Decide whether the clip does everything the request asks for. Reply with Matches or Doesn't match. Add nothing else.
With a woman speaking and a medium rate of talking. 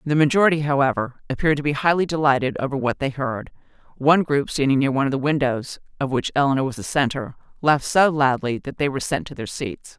Doesn't match